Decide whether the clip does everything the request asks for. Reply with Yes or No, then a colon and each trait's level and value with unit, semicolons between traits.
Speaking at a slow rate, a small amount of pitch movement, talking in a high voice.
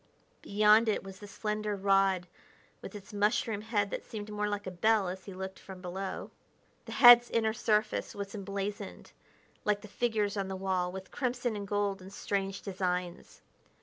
No: average, 175 wpm; narrow, 1.8 semitones; high, 205 Hz